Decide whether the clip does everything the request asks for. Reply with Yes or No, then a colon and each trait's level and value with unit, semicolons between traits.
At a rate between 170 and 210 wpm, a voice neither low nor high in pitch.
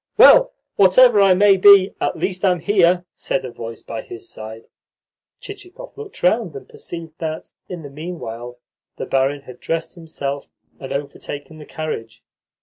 No: average, 155 wpm; medium, 165 Hz